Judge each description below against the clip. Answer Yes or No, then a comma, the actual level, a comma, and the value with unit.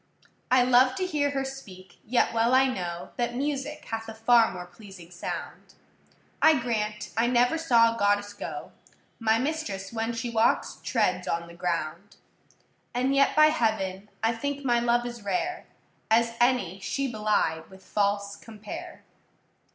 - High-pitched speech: Yes, high, 230 Hz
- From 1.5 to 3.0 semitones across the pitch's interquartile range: No, average, 4.1 semitones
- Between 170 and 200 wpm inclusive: No, average, 160 wpm